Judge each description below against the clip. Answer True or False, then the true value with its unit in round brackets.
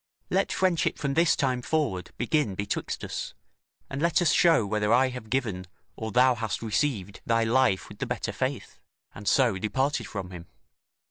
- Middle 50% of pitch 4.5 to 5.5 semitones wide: True (5.2 semitones)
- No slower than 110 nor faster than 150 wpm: False (175 wpm)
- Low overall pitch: True (120 Hz)